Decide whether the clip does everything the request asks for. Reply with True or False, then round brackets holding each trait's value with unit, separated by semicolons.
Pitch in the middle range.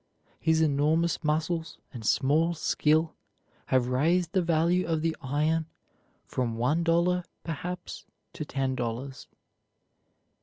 True (160 Hz)